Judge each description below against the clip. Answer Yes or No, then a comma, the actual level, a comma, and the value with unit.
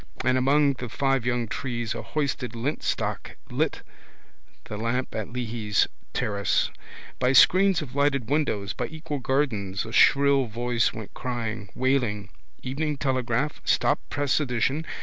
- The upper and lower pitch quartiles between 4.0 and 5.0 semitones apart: No, average, 3.5 semitones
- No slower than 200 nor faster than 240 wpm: No, slow, 135 wpm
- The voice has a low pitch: Yes, low, 125 Hz